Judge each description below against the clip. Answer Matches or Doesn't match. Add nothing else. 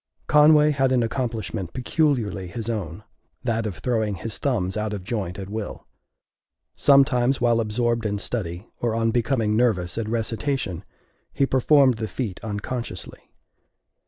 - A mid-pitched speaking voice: Doesn't match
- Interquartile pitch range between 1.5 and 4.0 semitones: Matches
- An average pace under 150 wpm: Matches